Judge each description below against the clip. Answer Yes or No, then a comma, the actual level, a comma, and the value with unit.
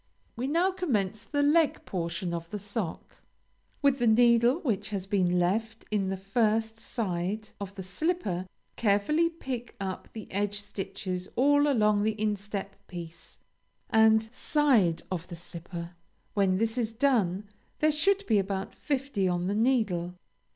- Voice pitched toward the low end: No, high, 210 Hz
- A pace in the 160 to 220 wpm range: No, average, 150 wpm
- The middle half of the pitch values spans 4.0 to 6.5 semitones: Yes, average, 4.6 semitones